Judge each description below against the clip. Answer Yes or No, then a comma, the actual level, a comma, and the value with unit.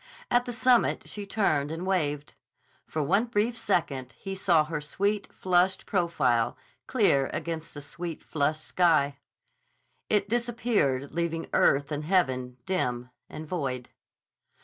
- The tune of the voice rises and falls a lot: Yes, wide, 5.7 semitones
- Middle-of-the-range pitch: Yes, medium, 165 Hz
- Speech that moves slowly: Yes, slow, 130 wpm